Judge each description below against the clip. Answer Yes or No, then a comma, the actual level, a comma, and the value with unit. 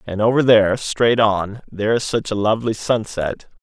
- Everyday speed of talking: Yes, average, 180 wpm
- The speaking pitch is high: No, low, 110 Hz